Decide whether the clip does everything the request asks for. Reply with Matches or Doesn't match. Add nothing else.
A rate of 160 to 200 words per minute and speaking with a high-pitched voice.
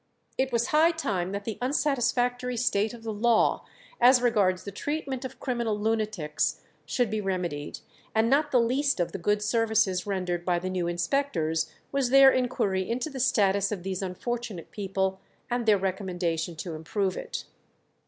Matches